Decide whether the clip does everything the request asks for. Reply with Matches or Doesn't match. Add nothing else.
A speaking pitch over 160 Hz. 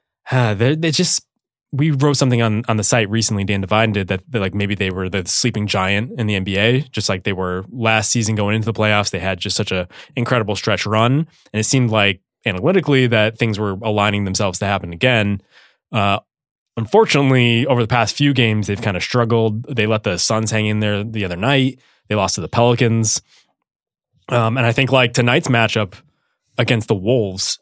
Doesn't match